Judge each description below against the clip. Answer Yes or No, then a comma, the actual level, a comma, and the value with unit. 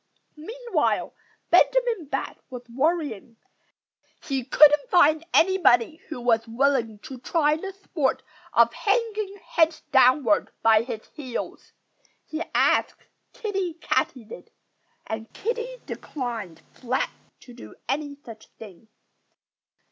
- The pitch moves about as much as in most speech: No, wide, 6.6 semitones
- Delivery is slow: Yes, slow, 110 wpm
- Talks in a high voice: Yes, very high, 285 Hz